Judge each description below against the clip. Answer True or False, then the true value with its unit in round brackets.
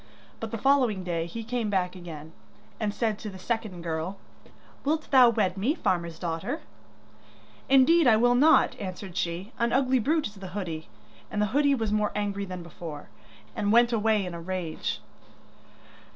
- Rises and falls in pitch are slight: False (5.1 semitones)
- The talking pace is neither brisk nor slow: True (170 wpm)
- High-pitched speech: True (205 Hz)